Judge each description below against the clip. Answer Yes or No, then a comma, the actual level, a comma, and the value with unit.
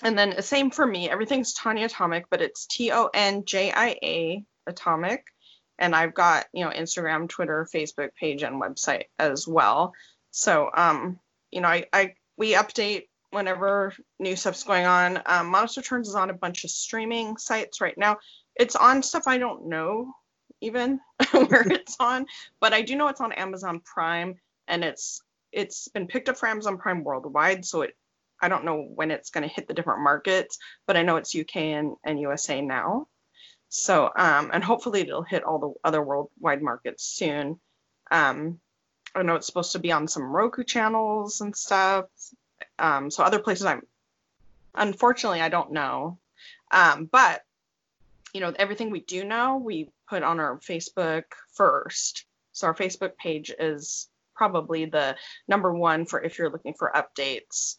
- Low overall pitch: No, high, 190 Hz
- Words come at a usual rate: Yes, average, 175 wpm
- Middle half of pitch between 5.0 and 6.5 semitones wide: Yes, average, 5.3 semitones